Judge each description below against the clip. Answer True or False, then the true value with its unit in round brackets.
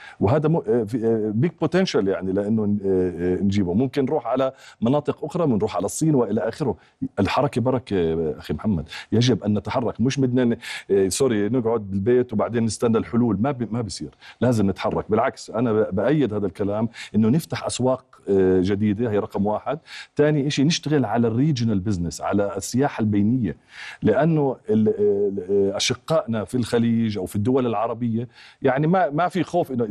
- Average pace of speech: False (155 wpm)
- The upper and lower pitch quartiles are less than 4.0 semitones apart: False (4.6 semitones)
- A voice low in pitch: True (115 Hz)